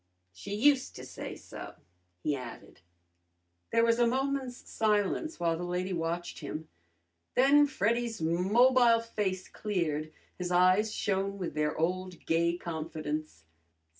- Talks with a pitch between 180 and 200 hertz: Yes, medium, 185 Hz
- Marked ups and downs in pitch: Yes, wide, 5.8 semitones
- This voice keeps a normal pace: No, slow, 130 wpm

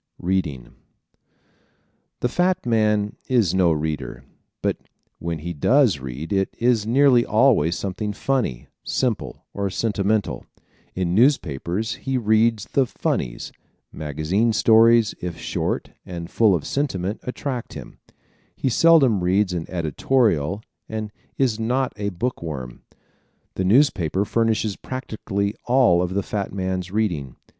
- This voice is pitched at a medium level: No, low, 105 Hz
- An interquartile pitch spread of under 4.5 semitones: No, average, 5.1 semitones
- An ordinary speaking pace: No, slow, 130 wpm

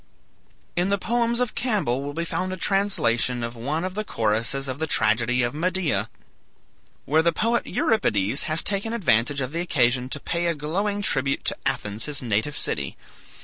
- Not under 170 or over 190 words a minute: Yes, average, 180 wpm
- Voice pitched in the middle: Yes, medium, 150 Hz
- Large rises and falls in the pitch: Yes, wide, 7.5 semitones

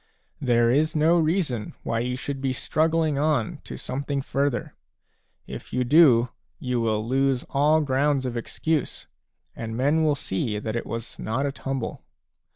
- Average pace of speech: Yes, average, 160 wpm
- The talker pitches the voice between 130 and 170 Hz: Yes, low, 135 Hz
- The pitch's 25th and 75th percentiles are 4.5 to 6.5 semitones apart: No, average, 3.9 semitones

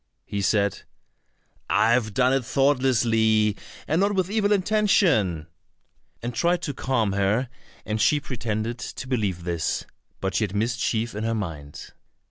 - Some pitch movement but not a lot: Yes, average, 4.8 semitones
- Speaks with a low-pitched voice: Yes, low, 115 Hz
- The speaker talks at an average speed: Yes, average, 145 wpm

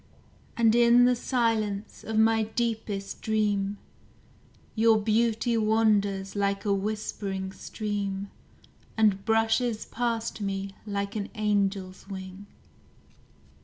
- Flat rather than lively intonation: Yes, narrow, 2.1 semitones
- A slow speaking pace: Yes, slow, 100 wpm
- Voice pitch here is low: No, high, 210 Hz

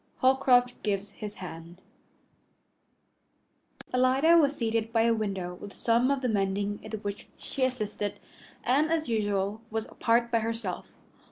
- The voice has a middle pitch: No, high, 225 Hz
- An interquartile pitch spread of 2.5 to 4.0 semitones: Yes, average, 3.7 semitones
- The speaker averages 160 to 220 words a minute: No, average, 140 wpm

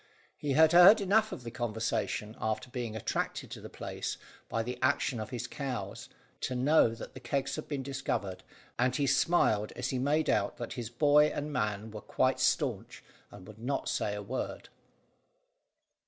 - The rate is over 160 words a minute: Yes, average, 180 wpm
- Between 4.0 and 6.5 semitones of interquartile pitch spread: Yes, average, 4.6 semitones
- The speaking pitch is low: Yes, low, 125 Hz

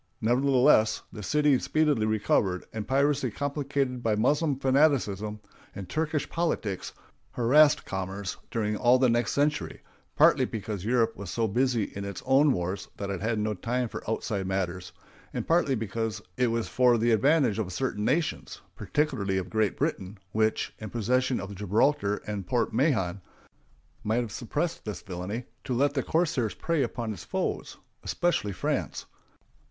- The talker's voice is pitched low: Yes, low, 115 Hz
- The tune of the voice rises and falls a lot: No, average, 4.9 semitones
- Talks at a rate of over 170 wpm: No, average, 155 wpm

